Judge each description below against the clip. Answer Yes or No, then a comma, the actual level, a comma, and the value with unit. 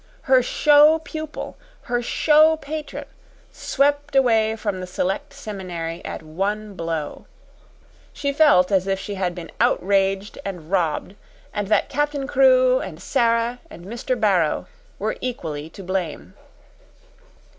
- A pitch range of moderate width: No, wide, 6.8 semitones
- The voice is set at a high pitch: Yes, high, 210 Hz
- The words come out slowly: Yes, slow, 130 wpm